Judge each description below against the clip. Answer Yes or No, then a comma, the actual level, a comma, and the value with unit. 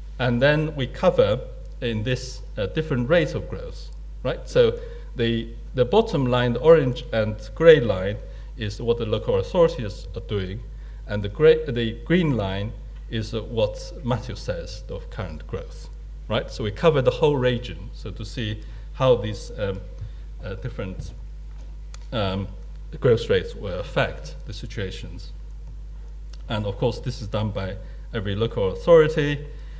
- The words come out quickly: No, average, 150 wpm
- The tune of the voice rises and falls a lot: Yes, wide, 5.8 semitones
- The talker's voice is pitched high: No, low, 120 Hz